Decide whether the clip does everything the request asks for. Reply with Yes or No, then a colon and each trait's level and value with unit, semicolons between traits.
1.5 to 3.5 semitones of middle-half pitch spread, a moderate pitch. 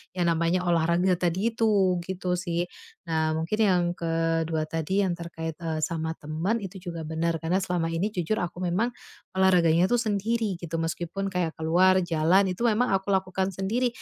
Yes: narrow, 2.6 semitones; medium, 175 Hz